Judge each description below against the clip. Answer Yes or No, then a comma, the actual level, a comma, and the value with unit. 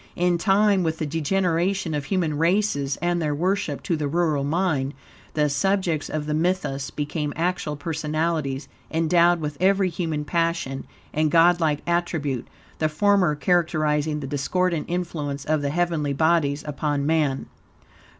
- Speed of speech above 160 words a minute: No, average, 140 wpm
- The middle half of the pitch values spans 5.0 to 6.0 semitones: No, average, 2.9 semitones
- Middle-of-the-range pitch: Yes, medium, 160 Hz